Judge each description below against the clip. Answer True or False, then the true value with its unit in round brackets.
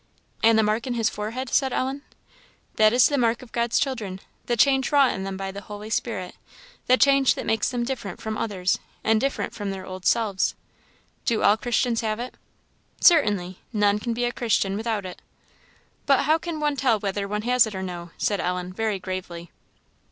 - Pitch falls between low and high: False (220 Hz)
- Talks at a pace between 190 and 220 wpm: True (195 wpm)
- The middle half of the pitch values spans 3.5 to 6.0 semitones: True (4.0 semitones)